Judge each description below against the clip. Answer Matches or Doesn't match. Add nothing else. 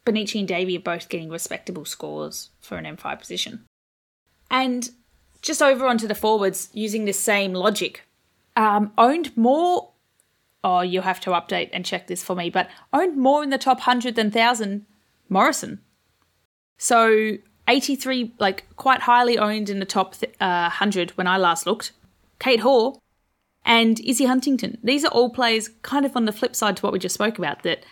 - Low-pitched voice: Doesn't match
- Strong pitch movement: Doesn't match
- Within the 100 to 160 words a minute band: Doesn't match